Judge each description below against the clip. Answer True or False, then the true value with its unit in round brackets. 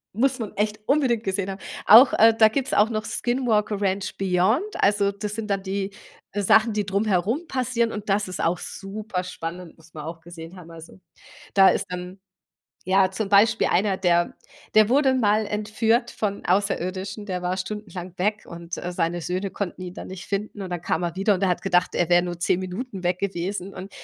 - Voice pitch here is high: True (195 Hz)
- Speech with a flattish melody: False (3.0 semitones)